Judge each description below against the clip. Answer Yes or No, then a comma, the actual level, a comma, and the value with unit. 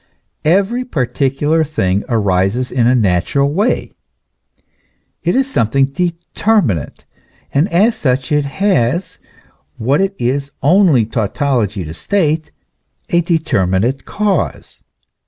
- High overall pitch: No, medium, 140 Hz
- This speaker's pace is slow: Yes, slow, 105 wpm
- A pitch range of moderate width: No, wide, 7.0 semitones